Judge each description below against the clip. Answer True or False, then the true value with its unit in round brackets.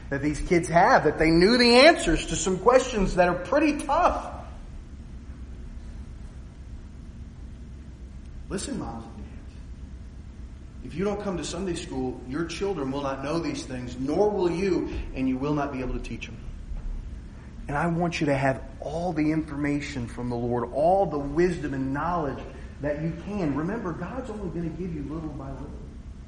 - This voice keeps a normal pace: True (175 wpm)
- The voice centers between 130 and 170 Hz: True (140 Hz)